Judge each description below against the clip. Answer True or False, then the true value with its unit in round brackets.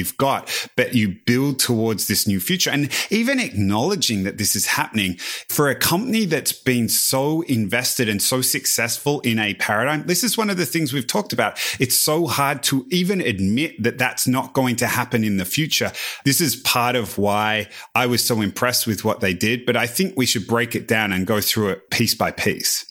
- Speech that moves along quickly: True (210 wpm)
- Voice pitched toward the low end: True (125 Hz)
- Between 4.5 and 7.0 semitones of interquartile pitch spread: True (4.8 semitones)